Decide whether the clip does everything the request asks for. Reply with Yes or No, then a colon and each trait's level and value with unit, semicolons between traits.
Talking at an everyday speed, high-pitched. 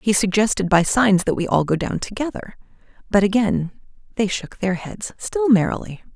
Yes: average, 175 wpm; high, 205 Hz